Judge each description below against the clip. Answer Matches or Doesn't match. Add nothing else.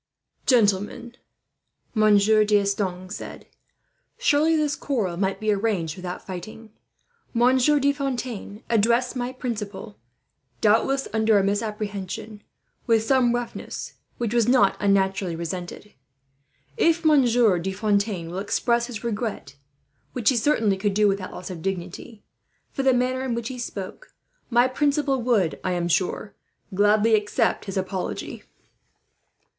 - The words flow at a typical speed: Doesn't match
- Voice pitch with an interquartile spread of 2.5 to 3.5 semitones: Doesn't match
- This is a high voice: Matches